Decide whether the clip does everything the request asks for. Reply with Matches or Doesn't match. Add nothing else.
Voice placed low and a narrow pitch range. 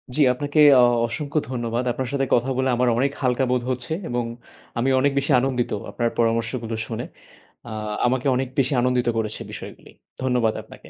Matches